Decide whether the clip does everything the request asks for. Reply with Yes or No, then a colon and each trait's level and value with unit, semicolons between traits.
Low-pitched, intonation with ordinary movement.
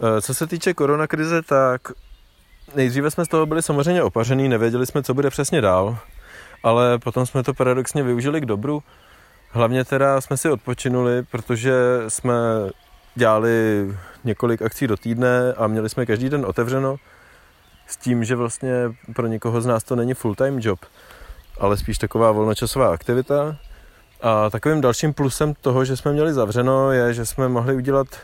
Yes: low, 125 Hz; average, 3.1 semitones